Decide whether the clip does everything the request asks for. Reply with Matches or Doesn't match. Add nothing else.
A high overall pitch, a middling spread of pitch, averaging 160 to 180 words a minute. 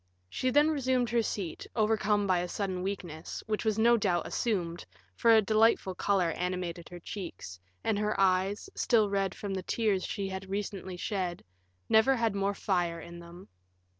Matches